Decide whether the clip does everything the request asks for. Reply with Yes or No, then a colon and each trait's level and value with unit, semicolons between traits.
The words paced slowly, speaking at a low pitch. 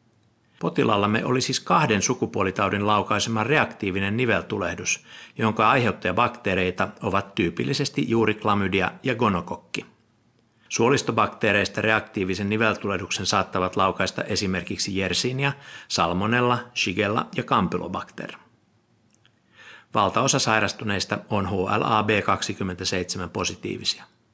Yes: slow, 75 wpm; low, 105 Hz